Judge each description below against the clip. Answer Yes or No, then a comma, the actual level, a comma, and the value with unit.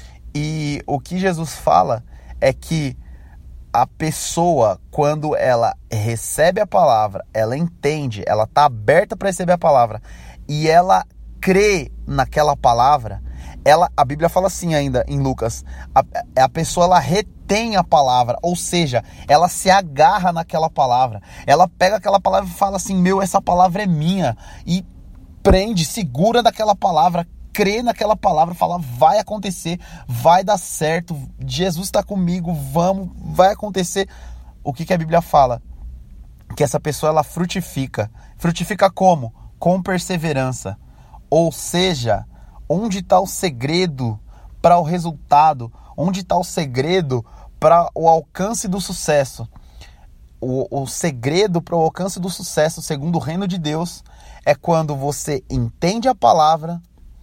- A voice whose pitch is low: No, medium, 165 Hz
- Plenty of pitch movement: Yes, wide, 5.8 semitones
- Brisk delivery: No, average, 140 wpm